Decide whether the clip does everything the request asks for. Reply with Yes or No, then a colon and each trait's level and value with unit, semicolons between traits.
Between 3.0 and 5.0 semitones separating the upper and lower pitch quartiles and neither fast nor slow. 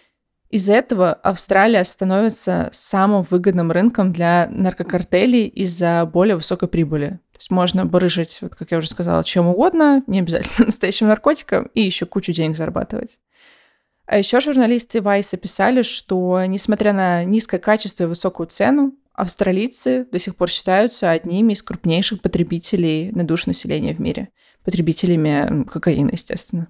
Yes: average, 3.6 semitones; average, 140 wpm